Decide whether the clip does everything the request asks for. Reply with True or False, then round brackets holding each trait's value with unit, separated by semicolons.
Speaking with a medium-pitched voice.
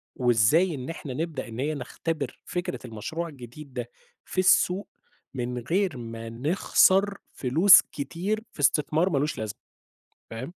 True (145 Hz)